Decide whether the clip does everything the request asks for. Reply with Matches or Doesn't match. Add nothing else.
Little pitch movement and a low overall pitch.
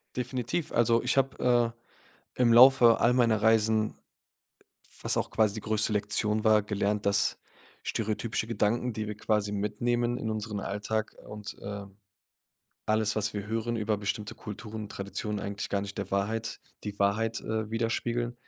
Matches